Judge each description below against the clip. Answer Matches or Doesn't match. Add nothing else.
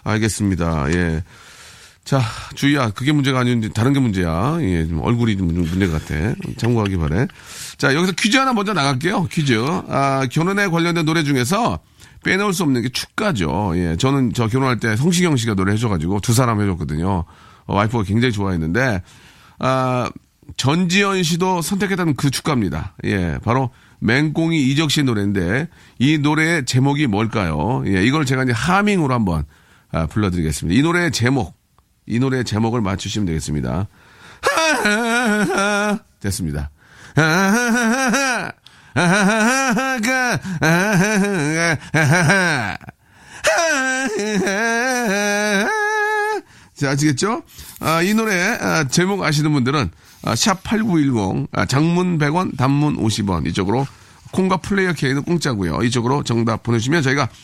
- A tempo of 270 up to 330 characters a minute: Matches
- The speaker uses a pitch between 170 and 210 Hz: Doesn't match